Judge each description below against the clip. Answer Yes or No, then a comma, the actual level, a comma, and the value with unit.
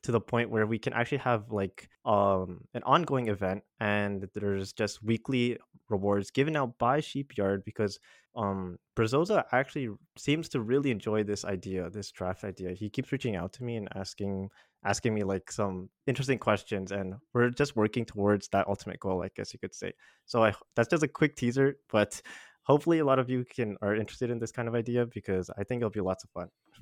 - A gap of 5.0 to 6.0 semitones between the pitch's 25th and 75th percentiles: No, average, 4.2 semitones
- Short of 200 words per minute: No, fast, 205 wpm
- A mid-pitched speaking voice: No, low, 110 Hz